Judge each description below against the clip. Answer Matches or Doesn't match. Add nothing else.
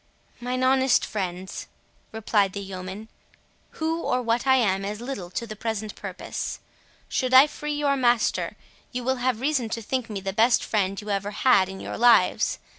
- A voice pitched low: Doesn't match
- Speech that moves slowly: Doesn't match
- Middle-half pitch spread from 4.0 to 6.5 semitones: Matches